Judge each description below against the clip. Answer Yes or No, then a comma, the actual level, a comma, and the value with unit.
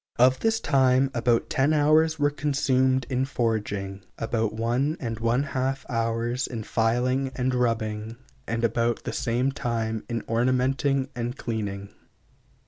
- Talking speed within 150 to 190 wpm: No, slow, 135 wpm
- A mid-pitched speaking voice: No, low, 125 Hz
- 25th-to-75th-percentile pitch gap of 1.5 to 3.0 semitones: Yes, average, 2.7 semitones